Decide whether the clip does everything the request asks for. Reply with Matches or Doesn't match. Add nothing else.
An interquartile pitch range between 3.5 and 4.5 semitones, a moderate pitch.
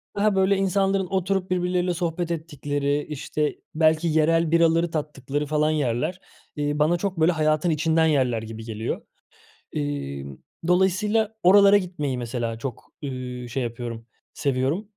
Doesn't match